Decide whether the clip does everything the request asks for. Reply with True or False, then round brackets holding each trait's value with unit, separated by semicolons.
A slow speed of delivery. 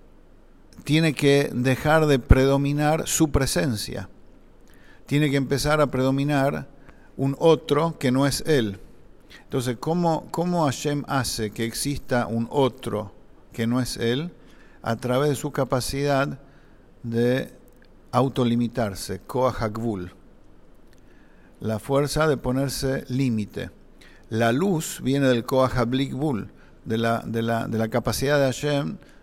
True (120 wpm)